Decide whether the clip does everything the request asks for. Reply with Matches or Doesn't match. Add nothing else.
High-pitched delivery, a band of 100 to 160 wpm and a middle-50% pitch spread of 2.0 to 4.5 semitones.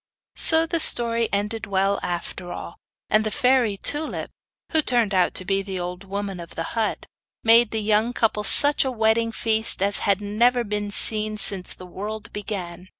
Doesn't match